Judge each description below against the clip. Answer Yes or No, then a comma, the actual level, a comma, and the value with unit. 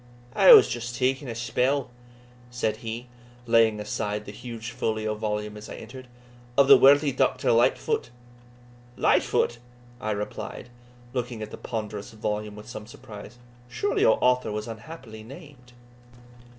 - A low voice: Yes, low, 115 Hz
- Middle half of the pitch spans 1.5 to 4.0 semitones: Yes, average, 2.7 semitones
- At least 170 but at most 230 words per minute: No, average, 140 wpm